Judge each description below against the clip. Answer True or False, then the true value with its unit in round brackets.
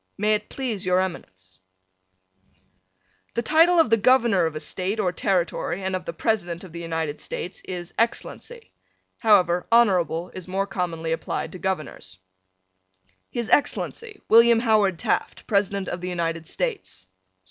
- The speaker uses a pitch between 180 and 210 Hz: True (190 Hz)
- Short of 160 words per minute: True (145 wpm)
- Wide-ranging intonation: False (4.7 semitones)